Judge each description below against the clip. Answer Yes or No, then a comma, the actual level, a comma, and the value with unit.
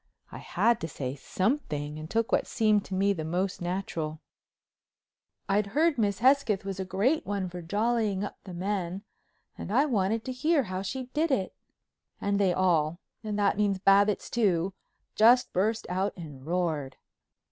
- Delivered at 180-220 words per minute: No, average, 160 wpm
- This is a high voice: Yes, high, 195 Hz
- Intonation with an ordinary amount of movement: Yes, average, 3.8 semitones